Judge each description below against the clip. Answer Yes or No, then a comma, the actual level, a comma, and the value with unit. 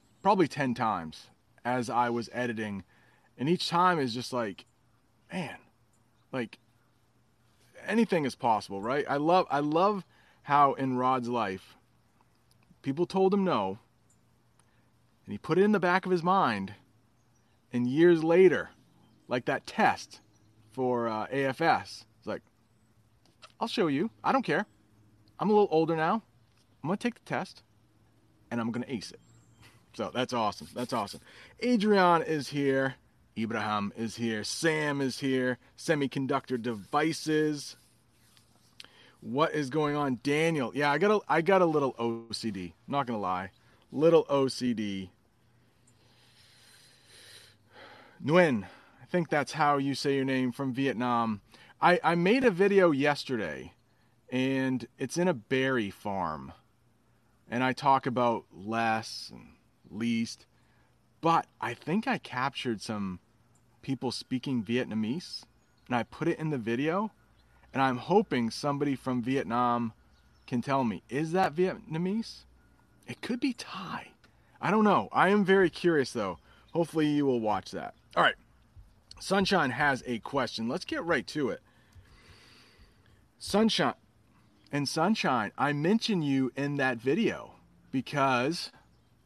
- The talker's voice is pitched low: Yes, low, 125 Hz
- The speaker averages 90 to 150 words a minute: Yes, average, 140 wpm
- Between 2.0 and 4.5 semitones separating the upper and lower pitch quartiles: No, average, 4.9 semitones